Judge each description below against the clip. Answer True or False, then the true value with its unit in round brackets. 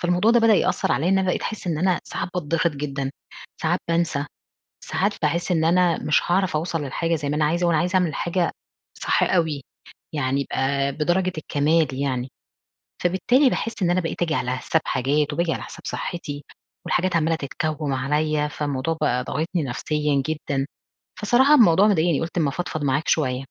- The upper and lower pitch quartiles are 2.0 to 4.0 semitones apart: True (3.6 semitones)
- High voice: False (160 Hz)